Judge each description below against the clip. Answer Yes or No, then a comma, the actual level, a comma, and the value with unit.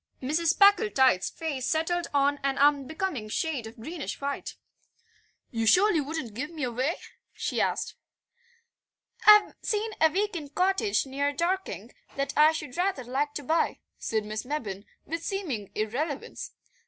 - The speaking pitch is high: Yes, very high, 295 Hz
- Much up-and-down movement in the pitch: No, average, 4.8 semitones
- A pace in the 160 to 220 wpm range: No, average, 140 wpm